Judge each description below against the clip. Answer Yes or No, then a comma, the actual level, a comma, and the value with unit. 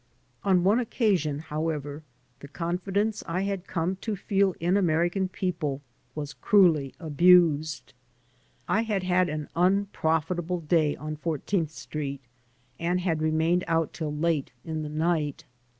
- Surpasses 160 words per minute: No, slow, 135 wpm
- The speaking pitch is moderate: Yes, medium, 165 Hz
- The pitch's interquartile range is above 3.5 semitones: No, average, 3.2 semitones